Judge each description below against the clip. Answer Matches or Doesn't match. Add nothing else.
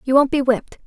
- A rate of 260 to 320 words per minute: Matches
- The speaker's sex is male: Doesn't match